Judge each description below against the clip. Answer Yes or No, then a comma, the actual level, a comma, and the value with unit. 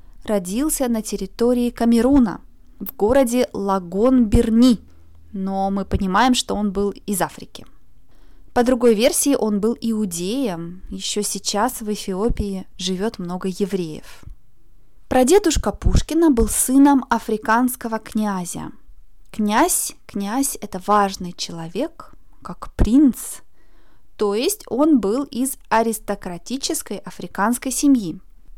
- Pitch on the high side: Yes, high, 220 Hz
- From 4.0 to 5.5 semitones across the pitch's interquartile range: Yes, average, 4.7 semitones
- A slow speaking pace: Yes, slow, 105 wpm